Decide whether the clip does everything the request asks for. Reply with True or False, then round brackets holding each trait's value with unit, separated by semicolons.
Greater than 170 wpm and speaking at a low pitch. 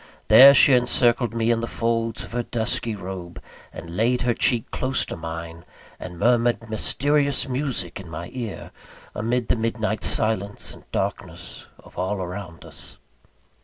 False (160 wpm; 115 Hz)